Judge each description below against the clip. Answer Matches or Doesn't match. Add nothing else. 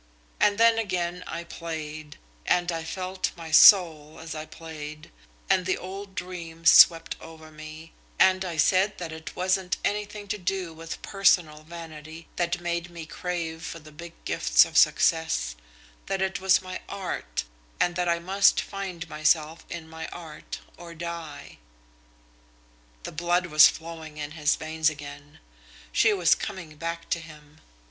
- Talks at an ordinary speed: Matches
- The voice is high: Doesn't match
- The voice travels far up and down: Doesn't match